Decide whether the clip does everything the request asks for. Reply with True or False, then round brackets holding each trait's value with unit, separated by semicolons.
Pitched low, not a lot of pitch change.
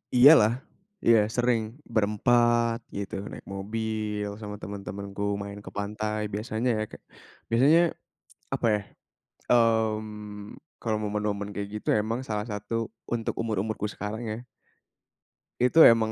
True (110 Hz; 1.8 semitones)